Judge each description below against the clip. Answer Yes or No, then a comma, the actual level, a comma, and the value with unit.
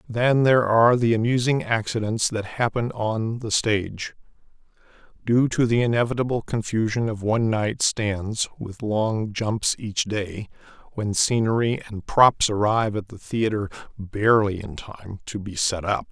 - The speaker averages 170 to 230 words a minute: No, average, 150 wpm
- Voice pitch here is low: Yes, low, 110 Hz